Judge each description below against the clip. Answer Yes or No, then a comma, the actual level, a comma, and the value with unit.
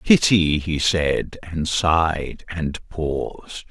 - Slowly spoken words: Yes, slow, 115 wpm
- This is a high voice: No, very low, 80 Hz